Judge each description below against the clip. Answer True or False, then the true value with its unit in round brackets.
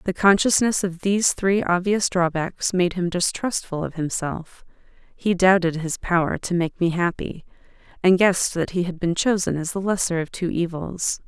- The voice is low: False (180 Hz)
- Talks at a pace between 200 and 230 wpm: False (175 wpm)